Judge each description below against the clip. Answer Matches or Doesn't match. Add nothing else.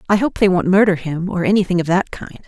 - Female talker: Matches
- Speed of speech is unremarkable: Doesn't match